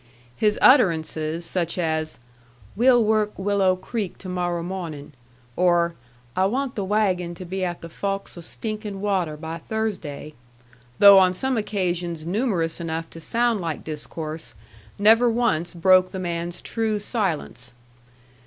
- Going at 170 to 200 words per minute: No, average, 140 wpm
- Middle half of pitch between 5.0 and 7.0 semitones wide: No, average, 3.9 semitones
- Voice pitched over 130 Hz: Yes, medium, 185 Hz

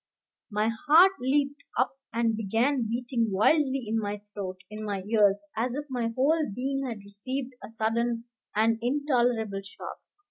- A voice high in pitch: Yes, high, 230 Hz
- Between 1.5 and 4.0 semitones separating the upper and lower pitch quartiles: Yes, average, 3.7 semitones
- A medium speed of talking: Yes, average, 150 wpm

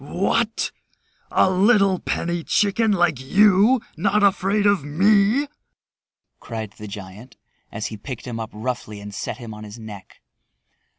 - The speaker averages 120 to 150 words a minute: Yes, average, 140 wpm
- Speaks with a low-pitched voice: No, medium, 165 Hz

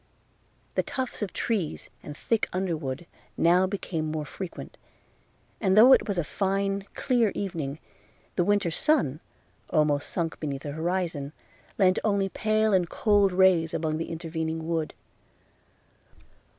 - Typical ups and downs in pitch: Yes, average, 4.0 semitones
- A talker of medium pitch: Yes, medium, 180 Hz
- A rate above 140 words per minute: No, slow, 135 wpm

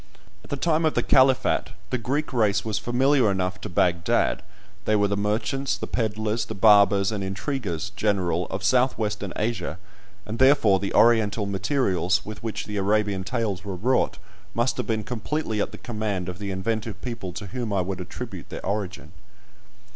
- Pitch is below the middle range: Yes, low, 105 Hz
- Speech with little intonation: No, average, 3.3 semitones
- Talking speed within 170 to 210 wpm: Yes, average, 175 wpm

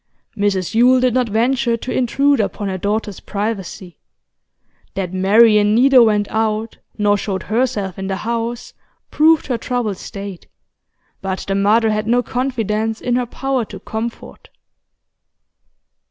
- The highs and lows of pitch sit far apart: No, average, 3.3 semitones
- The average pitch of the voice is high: Yes, high, 220 Hz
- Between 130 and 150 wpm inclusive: Yes, average, 140 wpm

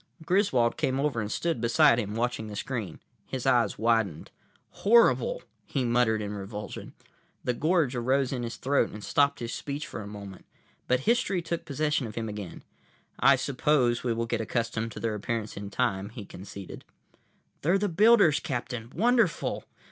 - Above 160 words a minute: Yes, average, 170 wpm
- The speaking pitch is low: Yes, low, 120 Hz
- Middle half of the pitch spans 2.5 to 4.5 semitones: No, average, 5.3 semitones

